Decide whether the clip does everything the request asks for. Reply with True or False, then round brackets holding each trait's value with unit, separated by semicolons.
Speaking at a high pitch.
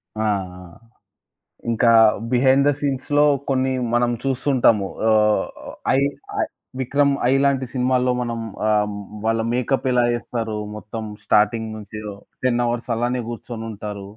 False (120 Hz)